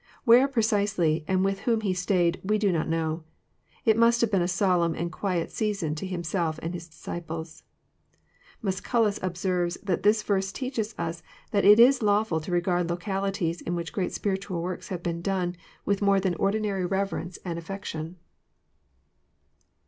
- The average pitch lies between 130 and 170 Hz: No, medium, 185 Hz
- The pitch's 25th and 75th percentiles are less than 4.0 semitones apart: Yes, average, 3.0 semitones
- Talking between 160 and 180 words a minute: Yes, average, 165 wpm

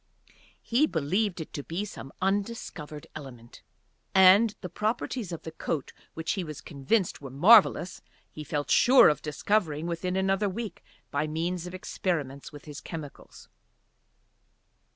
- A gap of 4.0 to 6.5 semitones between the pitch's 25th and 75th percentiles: Yes, average, 4.8 semitones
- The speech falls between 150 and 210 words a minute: No, average, 140 wpm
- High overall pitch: No, medium, 170 Hz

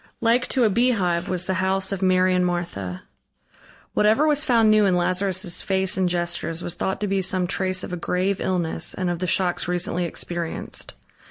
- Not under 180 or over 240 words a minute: Yes, average, 190 wpm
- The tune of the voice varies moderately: No, narrow, 1.9 semitones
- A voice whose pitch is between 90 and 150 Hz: No, medium, 185 Hz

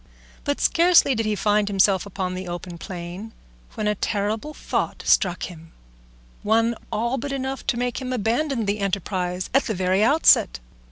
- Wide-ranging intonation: No, average, 5.0 semitones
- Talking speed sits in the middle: Yes, average, 165 wpm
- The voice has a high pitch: Yes, high, 210 Hz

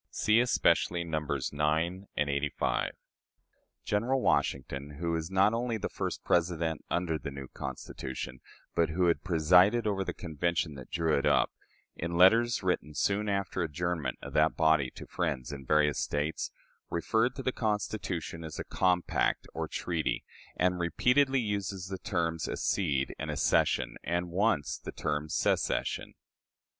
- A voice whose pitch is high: No, very low, 85 Hz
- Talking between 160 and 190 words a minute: No, average, 150 wpm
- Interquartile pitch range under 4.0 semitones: No, average, 4.4 semitones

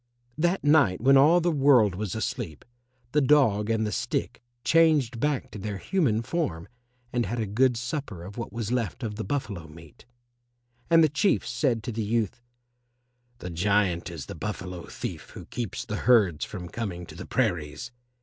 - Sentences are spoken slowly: No, average, 180 wpm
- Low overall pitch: Yes, low, 115 Hz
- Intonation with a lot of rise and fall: Yes, wide, 6.0 semitones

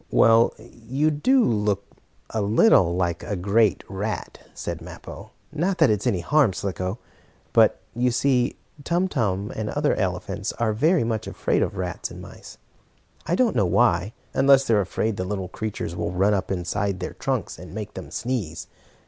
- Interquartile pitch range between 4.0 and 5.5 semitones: Yes, average, 4.9 semitones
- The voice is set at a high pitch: No, low, 110 Hz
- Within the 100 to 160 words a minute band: No, average, 175 wpm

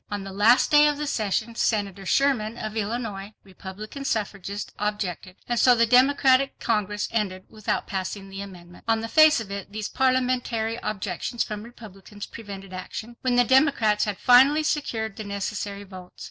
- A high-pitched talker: Yes, high, 215 Hz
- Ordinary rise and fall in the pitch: Yes, average, 3.6 semitones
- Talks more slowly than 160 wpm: No, average, 165 wpm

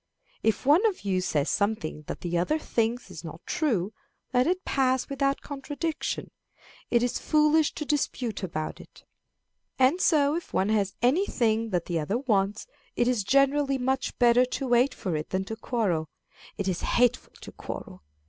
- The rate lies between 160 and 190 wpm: Yes, average, 175 wpm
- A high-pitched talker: Yes, high, 245 Hz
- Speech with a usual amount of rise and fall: No, wide, 6.0 semitones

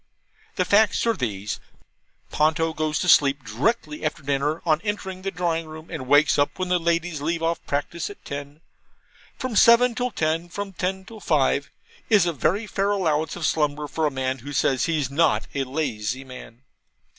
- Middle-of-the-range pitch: Yes, medium, 155 Hz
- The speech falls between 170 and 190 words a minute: Yes, average, 180 wpm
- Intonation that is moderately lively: Yes, average, 4.3 semitones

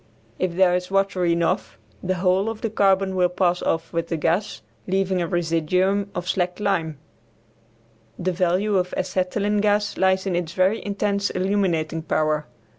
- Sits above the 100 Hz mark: Yes, medium, 185 Hz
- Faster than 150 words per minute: Yes, average, 160 wpm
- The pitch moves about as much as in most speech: No, narrow, 2.2 semitones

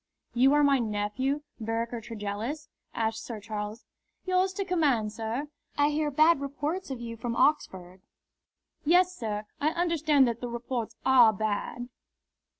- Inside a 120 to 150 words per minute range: Yes, average, 145 wpm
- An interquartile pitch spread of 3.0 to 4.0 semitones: No, average, 5.1 semitones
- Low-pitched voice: No, high, 245 Hz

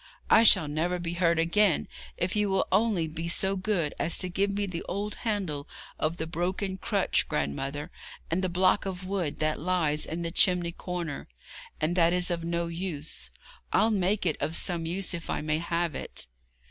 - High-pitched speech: No, medium, 175 Hz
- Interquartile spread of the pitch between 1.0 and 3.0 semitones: Yes, narrow, 2.6 semitones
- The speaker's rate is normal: Yes, average, 190 wpm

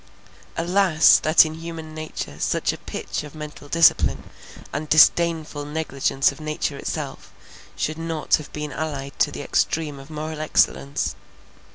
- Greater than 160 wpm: No, average, 145 wpm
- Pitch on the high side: No, medium, 155 Hz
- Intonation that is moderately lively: No, narrow, 1.4 semitones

